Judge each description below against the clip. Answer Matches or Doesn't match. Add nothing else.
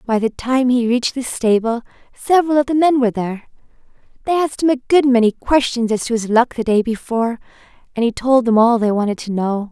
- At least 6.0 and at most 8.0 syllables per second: Matches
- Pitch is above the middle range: Matches